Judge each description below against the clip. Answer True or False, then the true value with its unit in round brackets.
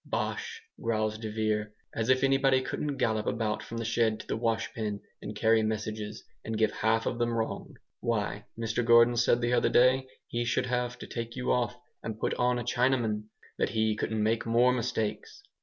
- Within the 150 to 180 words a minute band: False (190 wpm)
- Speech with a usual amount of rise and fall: False (2.0 semitones)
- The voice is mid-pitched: False (115 Hz)